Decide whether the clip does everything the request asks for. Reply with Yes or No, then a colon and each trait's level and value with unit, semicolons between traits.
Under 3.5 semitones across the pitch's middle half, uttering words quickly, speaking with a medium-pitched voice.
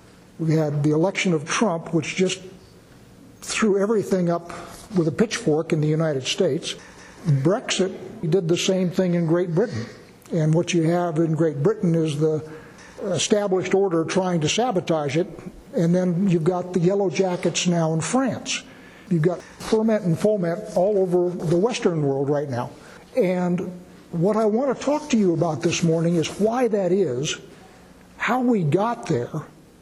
No: average, 2.9 semitones; average, 165 wpm; medium, 180 Hz